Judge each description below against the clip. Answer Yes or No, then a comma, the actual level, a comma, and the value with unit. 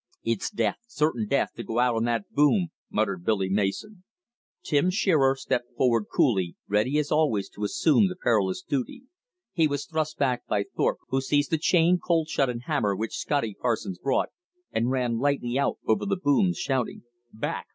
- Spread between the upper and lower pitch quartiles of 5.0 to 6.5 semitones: Yes, wide, 5.5 semitones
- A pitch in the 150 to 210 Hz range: No, low, 130 Hz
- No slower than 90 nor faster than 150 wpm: No, average, 180 wpm